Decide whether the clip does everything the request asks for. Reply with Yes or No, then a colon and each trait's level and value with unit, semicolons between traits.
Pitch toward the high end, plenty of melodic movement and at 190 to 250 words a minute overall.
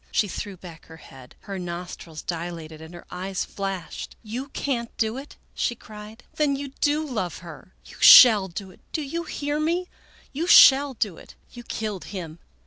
Yes: high, 210 Hz; wide, 7.6 semitones; average, 195 wpm